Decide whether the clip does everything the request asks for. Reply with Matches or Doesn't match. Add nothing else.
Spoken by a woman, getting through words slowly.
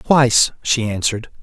Doesn't match